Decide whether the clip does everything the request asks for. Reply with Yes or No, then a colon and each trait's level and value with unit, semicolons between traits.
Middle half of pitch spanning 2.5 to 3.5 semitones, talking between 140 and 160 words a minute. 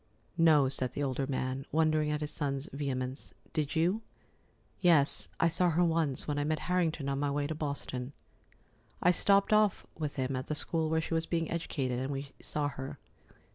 No: average, 3.0 semitones; average, 190 wpm